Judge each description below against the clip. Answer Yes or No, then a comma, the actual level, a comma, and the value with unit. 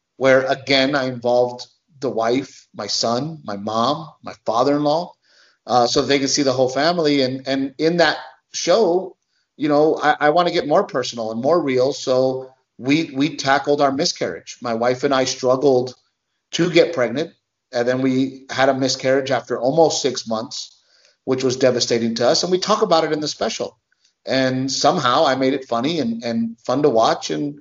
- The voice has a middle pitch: No, low, 130 Hz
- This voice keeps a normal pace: Yes, average, 185 wpm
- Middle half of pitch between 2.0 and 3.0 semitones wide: Yes, narrow, 2.6 semitones